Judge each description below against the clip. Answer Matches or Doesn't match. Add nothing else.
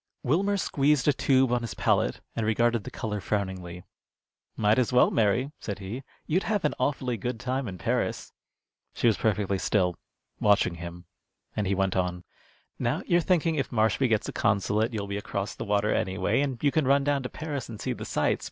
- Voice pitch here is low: Matches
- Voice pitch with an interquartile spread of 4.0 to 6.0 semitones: Matches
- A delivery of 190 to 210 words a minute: Matches